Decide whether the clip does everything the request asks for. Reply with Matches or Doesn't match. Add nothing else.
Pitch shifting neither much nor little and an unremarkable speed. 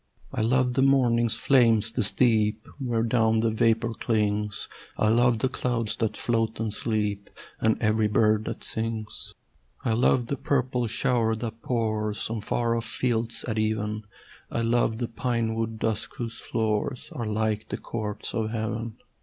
Doesn't match